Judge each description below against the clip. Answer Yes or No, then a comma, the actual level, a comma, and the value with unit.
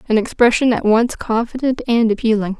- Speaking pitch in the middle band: No, high, 230 Hz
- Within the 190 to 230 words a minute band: No, average, 160 wpm